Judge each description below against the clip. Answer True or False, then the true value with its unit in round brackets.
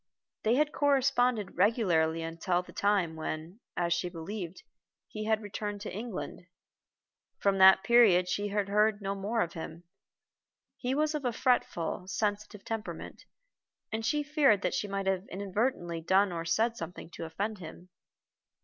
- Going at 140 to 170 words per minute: True (150 wpm)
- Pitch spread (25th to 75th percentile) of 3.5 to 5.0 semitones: True (4.1 semitones)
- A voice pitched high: True (200 Hz)